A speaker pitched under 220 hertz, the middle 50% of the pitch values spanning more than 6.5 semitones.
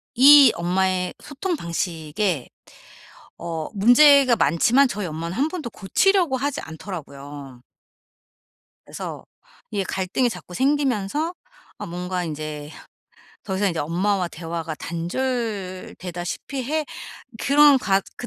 Yes: high, 190 Hz; wide, 7.7 semitones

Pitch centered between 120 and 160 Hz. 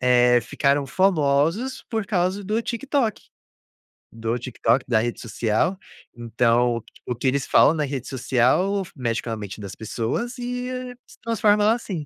Yes: medium, 140 Hz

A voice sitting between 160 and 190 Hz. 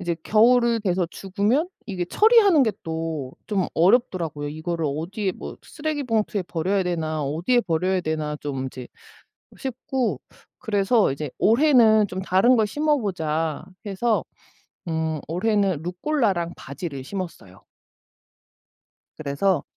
Yes: medium, 185 Hz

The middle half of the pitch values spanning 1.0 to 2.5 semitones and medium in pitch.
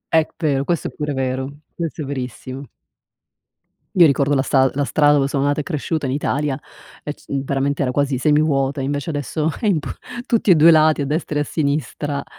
Yes: narrow, 2.1 semitones; medium, 145 Hz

